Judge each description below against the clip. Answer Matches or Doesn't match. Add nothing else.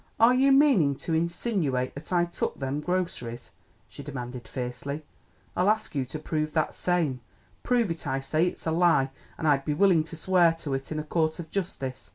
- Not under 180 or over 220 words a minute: Matches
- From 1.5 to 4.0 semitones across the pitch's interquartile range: Doesn't match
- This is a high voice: Doesn't match